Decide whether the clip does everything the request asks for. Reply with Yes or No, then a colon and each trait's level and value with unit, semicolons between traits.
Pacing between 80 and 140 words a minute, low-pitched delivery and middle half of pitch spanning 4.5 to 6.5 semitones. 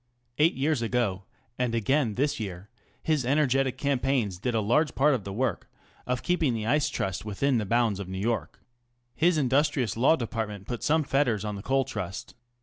No: average, 180 wpm; low, 125 Hz; average, 4.8 semitones